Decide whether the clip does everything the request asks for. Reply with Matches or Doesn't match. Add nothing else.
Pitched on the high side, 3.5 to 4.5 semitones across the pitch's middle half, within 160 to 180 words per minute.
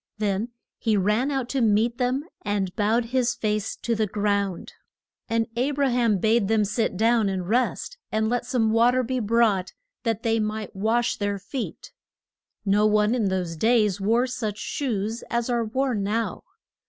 Doesn't match